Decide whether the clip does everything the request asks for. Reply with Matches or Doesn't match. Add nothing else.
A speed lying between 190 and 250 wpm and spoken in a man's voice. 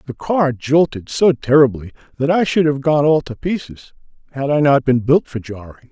Matches